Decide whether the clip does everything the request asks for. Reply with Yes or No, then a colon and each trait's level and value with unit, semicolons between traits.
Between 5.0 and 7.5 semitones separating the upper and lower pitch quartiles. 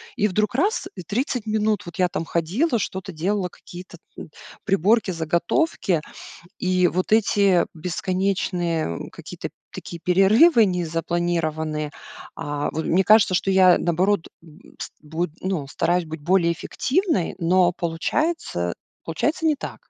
No: average, 3.7 semitones